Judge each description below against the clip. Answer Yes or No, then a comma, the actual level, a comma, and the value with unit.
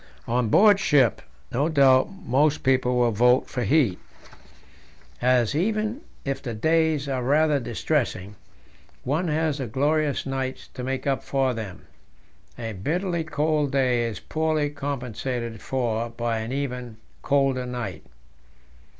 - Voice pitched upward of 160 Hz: No, low, 135 Hz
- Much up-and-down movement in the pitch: No, average, 3.8 semitones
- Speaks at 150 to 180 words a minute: No, slow, 135 wpm